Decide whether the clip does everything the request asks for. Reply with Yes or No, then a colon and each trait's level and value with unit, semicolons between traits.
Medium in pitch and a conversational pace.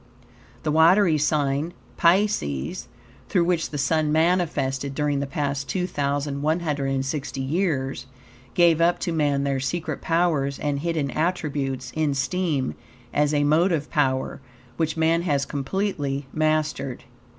No: medium, 150 Hz; slow, 120 wpm